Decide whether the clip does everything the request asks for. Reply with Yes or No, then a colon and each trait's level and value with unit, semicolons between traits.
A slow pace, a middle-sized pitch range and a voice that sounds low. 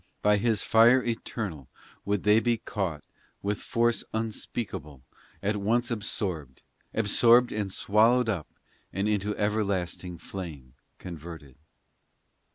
Yes: slow, 110 wpm; average, 4.3 semitones; low, 105 Hz